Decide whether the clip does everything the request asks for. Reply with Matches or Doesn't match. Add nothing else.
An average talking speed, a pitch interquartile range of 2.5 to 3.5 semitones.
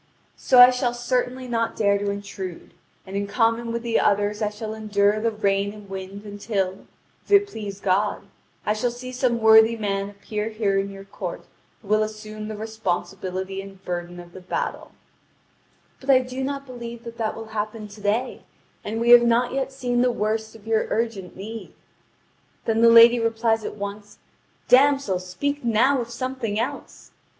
Matches